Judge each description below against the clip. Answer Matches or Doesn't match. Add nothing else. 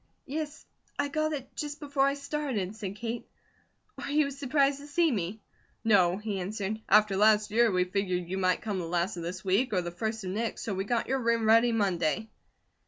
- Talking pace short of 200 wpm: Doesn't match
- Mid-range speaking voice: Doesn't match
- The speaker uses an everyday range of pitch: Doesn't match